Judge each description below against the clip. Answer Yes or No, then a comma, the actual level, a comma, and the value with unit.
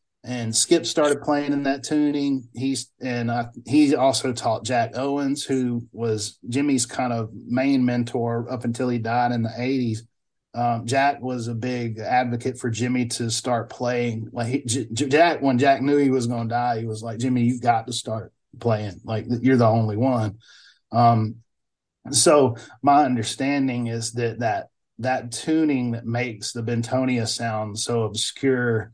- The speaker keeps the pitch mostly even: Yes, narrow, 2.3 semitones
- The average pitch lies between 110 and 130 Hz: Yes, low, 120 Hz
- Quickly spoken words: No, average, 175 wpm